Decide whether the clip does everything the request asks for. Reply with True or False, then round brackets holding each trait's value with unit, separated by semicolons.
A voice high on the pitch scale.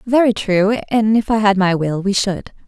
True (205 Hz)